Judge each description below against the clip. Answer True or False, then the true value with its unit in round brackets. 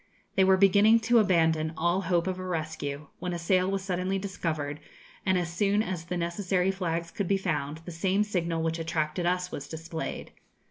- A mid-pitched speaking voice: True (180 Hz)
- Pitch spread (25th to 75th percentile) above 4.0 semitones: False (2.7 semitones)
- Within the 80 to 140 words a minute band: False (190 wpm)